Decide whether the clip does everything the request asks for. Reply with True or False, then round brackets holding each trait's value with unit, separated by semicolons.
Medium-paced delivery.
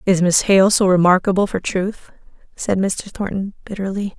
True (160 wpm)